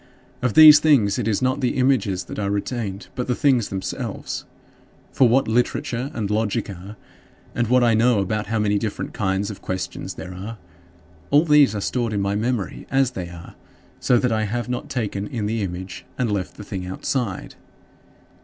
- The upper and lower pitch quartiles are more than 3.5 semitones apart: Yes, average, 4.0 semitones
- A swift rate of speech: No, average, 190 wpm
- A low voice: Yes, low, 110 Hz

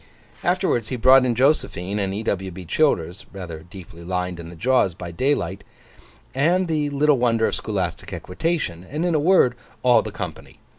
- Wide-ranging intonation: Yes, wide, 8.0 semitones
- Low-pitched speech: Yes, low, 110 Hz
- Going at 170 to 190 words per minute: Yes, average, 180 wpm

